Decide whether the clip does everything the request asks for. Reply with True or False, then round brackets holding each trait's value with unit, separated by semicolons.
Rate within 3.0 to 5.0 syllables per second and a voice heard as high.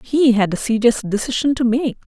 False (5.4 syllables/s; 240 Hz)